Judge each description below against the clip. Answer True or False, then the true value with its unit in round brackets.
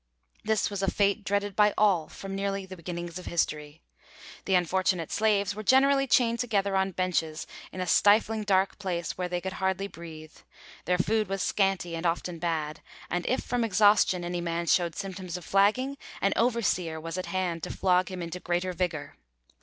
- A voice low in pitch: False (185 Hz)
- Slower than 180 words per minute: False (185 wpm)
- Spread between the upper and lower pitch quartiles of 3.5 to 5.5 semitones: False (2.7 semitones)